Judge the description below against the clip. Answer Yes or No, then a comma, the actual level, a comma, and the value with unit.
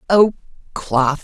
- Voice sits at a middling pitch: Yes, medium, 165 Hz